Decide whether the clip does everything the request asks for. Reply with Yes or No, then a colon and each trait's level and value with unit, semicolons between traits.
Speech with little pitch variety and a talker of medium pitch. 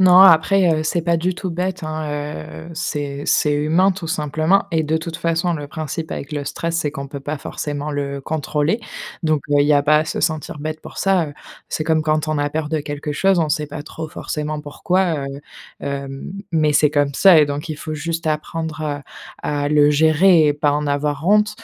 Yes: narrow, 2.1 semitones; medium, 155 Hz